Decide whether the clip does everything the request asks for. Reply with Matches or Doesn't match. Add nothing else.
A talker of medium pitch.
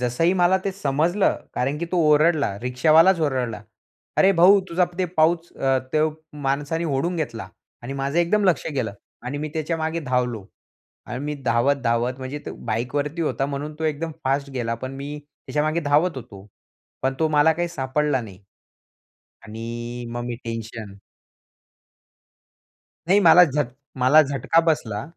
Matches